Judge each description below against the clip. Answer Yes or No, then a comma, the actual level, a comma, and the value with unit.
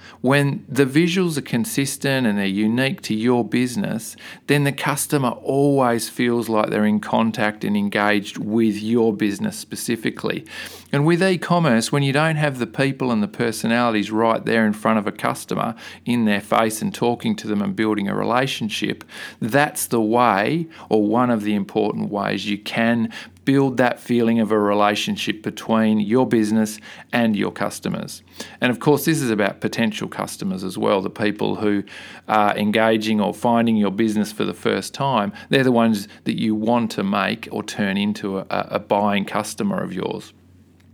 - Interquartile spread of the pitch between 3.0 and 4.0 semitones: Yes, average, 3.4 semitones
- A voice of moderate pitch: No, low, 115 Hz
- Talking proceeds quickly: No, average, 175 wpm